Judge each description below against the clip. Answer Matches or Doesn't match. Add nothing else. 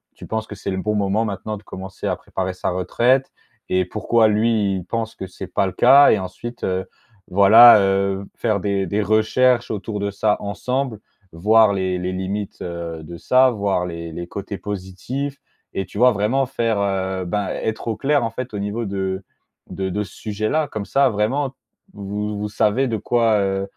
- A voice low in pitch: Matches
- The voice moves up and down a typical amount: Matches